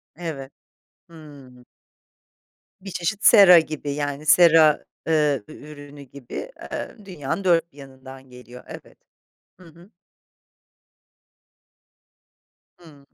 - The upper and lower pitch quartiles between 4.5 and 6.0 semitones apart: No, average, 3.5 semitones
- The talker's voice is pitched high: No, medium, 150 Hz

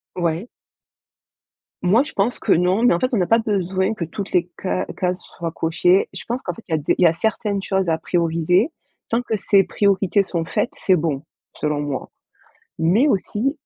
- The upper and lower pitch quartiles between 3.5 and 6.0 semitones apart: Yes, average, 4.3 semitones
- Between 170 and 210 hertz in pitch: Yes, medium, 185 Hz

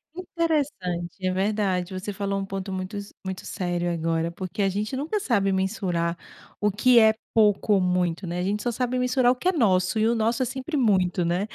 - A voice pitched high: Yes, high, 195 Hz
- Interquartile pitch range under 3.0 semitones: No, average, 4.1 semitones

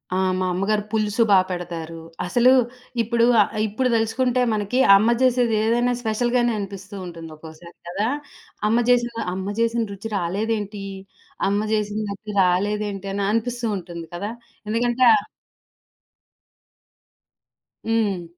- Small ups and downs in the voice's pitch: No, average, 3.6 semitones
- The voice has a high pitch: Yes, high, 210 Hz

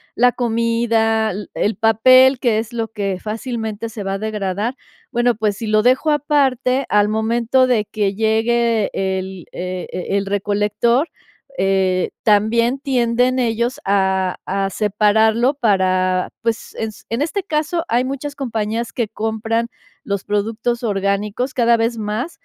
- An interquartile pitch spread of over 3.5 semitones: No, average, 2.8 semitones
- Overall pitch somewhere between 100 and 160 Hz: No, high, 225 Hz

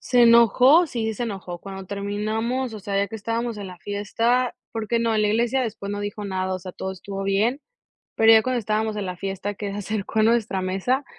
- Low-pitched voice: No, high, 215 Hz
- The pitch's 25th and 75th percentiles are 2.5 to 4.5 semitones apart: Yes, average, 2.9 semitones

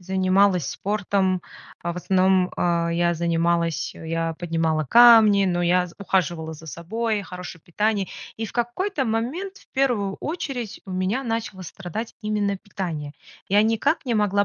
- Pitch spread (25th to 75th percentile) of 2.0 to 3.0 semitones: No, average, 4.4 semitones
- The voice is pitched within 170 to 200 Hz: Yes, high, 190 Hz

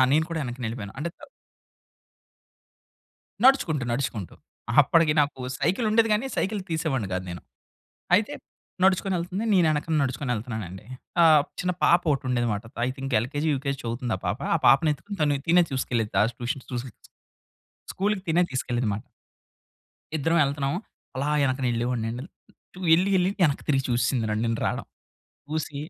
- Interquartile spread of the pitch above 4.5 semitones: Yes, wide, 5.6 semitones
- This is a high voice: No, medium, 140 Hz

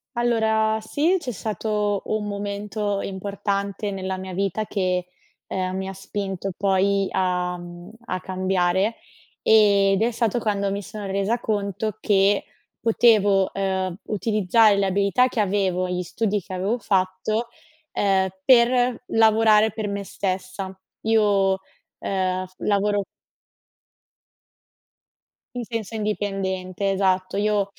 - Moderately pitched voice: No, high, 200 Hz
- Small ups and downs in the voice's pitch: Yes, narrow, 2.2 semitones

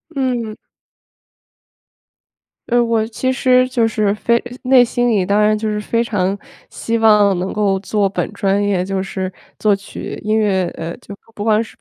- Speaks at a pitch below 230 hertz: Yes, high, 210 Hz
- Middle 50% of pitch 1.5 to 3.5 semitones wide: Yes, average, 2.8 semitones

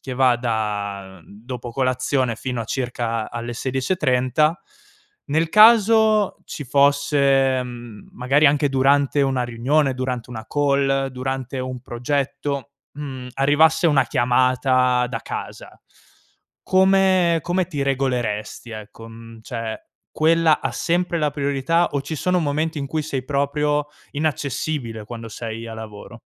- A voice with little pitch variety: No, average, 3.4 semitones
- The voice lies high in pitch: No, low, 135 Hz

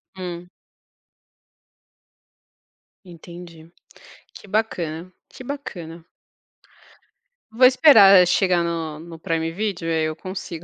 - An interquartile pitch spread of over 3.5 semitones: No, average, 2.9 semitones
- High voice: No, medium, 175 Hz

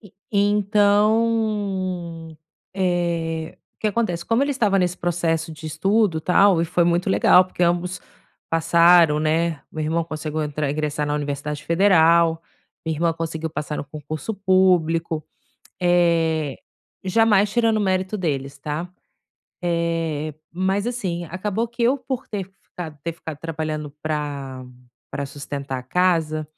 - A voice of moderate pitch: Yes, medium, 170 Hz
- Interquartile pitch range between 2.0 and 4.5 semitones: Yes, average, 3.6 semitones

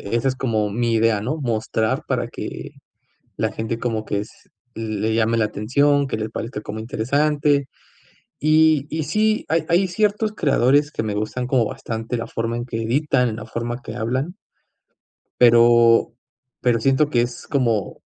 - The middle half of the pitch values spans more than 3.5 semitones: Yes, average, 4.2 semitones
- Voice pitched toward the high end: No, low, 120 Hz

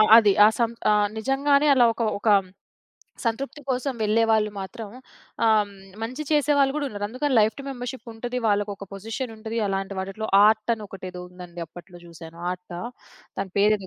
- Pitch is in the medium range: No, high, 220 Hz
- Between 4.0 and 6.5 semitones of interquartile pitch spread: Yes, average, 4.3 semitones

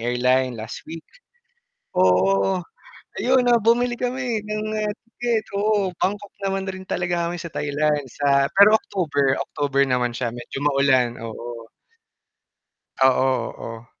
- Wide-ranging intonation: Yes, wide, 8.6 semitones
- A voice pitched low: No, medium, 145 Hz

